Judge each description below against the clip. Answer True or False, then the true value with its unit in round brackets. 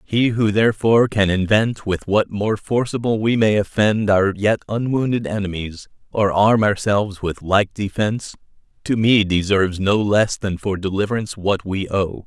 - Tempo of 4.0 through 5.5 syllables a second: True (4.9 syllables/s)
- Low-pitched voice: True (105 Hz)